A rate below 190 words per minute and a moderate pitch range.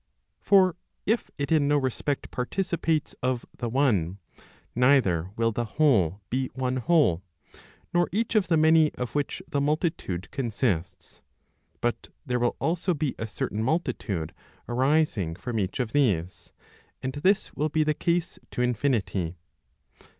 No: average, 145 wpm; wide, 5.8 semitones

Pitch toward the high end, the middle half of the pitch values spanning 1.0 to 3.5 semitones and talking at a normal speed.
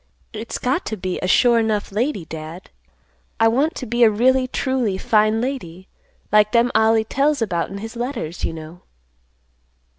No: high, 220 Hz; average, 4.4 semitones; average, 170 wpm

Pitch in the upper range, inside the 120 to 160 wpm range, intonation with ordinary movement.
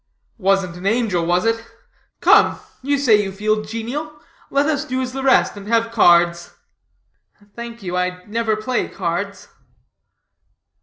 Yes: high, 215 Hz; average, 145 wpm; average, 4.7 semitones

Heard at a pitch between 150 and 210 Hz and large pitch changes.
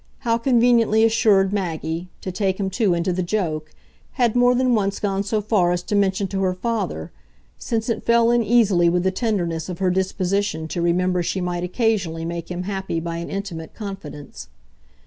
No: high, 190 Hz; average, 3.9 semitones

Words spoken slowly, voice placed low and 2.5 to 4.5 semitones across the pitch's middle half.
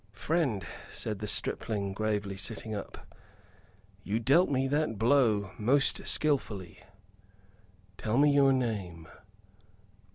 No: slow, 105 wpm; low, 110 Hz; average, 5.2 semitones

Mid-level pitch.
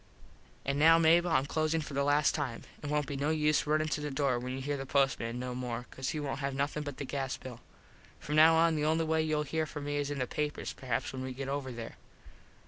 Yes: medium, 145 Hz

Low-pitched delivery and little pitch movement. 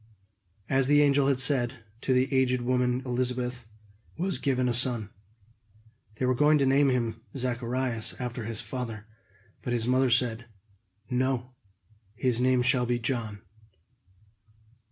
Yes: low, 125 Hz; narrow, 1.5 semitones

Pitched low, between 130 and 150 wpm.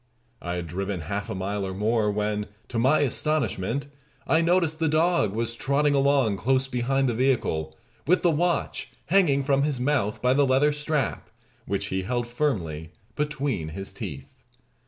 No: low, 125 Hz; average, 165 wpm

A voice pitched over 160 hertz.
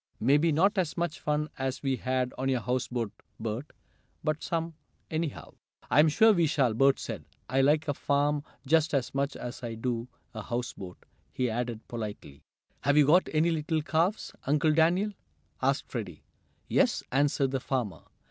No: medium, 140 Hz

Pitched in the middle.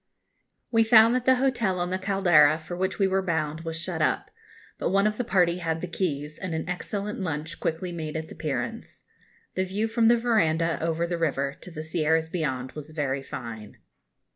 Yes: medium, 170 Hz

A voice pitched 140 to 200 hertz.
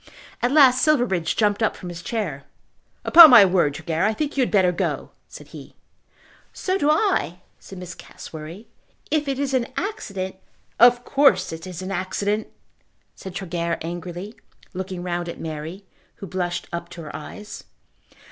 Yes: high, 190 Hz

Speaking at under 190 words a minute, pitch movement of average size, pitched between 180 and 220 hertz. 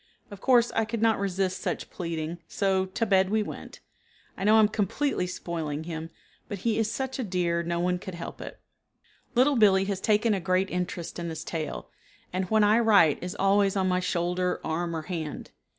No: average, 200 wpm; average, 3.5 semitones; high, 190 Hz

